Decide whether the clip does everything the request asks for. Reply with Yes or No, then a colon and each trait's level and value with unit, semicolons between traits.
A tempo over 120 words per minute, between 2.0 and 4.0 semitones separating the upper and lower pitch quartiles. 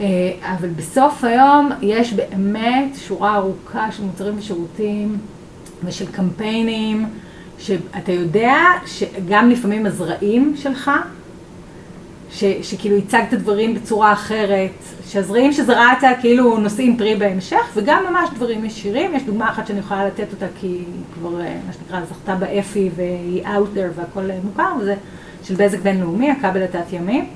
Yes: average, 130 wpm; average, 3.4 semitones